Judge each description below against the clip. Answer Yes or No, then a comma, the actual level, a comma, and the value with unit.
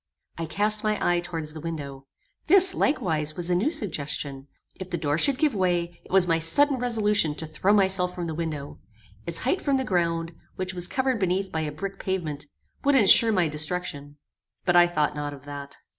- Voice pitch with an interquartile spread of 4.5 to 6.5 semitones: Yes, average, 5.0 semitones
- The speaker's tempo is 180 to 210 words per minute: Yes, average, 200 wpm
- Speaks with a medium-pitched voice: Yes, medium, 175 Hz